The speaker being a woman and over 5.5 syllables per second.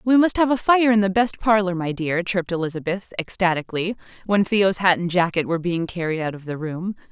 Yes: female; 5.8 syllables/s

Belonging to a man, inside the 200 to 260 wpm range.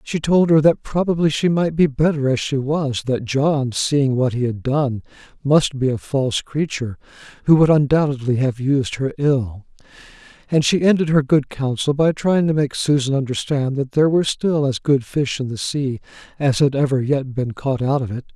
Yes: male; fast, 205 wpm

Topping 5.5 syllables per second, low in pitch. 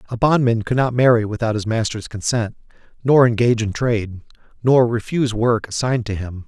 Yes: 5.7 syllables/s; low, 115 Hz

